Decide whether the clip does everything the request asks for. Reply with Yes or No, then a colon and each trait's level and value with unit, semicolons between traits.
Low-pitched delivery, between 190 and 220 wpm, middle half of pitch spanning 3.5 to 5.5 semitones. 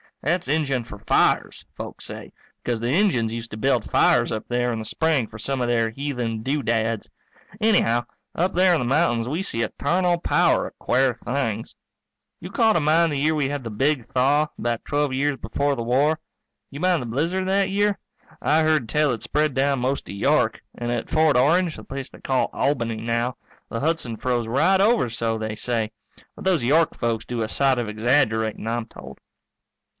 Yes: low, 130 Hz; average, 200 wpm; average, 5.1 semitones